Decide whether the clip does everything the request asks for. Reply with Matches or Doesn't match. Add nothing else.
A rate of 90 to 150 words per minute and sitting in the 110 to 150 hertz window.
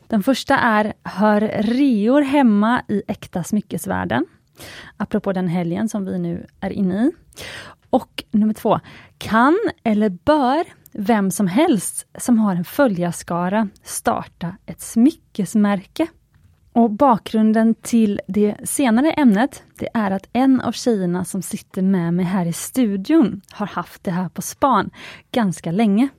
Doesn't match